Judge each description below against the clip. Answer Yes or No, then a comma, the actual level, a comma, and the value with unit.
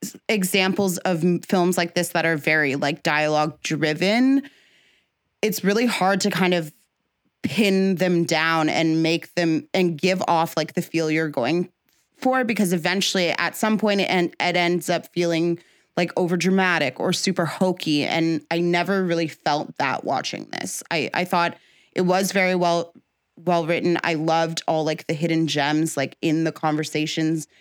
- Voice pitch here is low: No, medium, 175 Hz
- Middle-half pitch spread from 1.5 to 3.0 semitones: Yes, narrow, 2.4 semitones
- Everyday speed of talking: Yes, average, 165 wpm